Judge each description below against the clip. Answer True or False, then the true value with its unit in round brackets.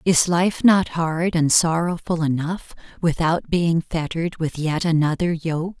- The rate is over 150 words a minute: False (145 wpm)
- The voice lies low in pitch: False (165 Hz)